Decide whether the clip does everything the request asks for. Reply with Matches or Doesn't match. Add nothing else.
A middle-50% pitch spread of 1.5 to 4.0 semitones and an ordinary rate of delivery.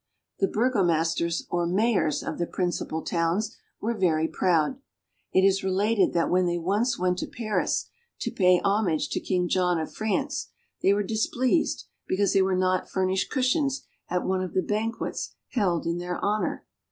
Matches